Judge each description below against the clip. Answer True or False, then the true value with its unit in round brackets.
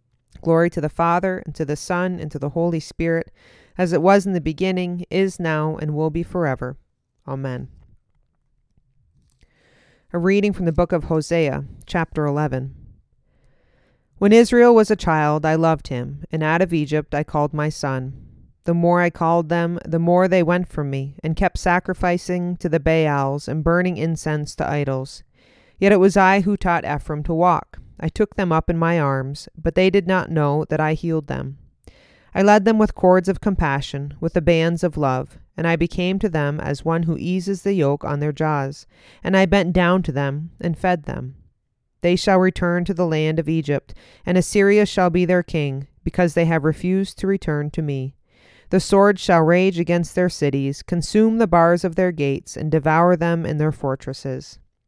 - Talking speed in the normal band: True (190 wpm)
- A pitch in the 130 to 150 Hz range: False (165 Hz)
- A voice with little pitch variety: False (3.3 semitones)